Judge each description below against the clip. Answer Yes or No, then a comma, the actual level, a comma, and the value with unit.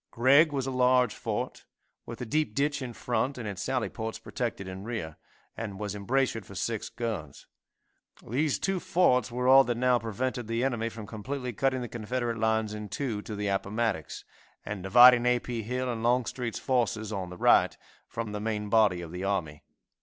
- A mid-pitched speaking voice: No, low, 115 Hz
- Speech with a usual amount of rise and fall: Yes, average, 3.3 semitones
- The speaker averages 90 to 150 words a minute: No, average, 190 wpm